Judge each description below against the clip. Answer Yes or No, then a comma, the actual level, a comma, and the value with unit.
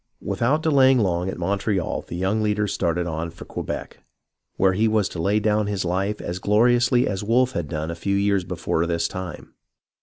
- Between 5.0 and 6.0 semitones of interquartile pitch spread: No, average, 3.7 semitones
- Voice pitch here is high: No, low, 100 Hz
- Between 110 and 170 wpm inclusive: No, average, 190 wpm